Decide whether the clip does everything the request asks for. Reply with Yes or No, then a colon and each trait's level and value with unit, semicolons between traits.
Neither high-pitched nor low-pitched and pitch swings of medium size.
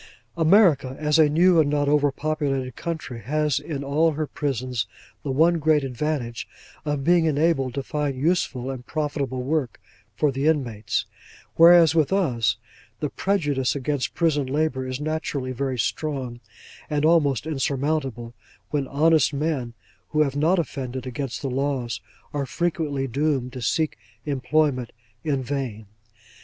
Yes: medium, 145 Hz; average, 3.2 semitones